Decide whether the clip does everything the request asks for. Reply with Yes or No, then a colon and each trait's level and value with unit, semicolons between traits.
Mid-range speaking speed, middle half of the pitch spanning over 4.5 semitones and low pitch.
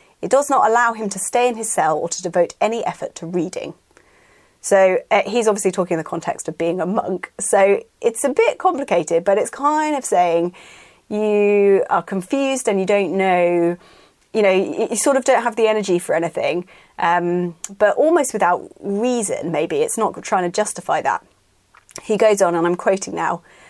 No: average, 195 wpm; average, 5.3 semitones; high, 200 Hz